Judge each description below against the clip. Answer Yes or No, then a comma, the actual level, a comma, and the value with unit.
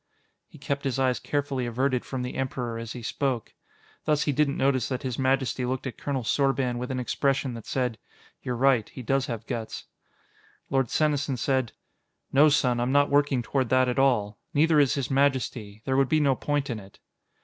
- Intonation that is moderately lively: No, narrow, 2.1 semitones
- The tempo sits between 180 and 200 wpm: Yes, average, 195 wpm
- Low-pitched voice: Yes, low, 130 Hz